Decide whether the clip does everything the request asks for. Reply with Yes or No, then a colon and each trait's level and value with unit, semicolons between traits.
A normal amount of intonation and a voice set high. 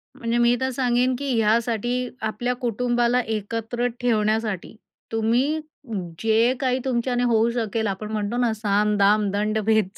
No: narrow, 2.2 semitones; high, 230 Hz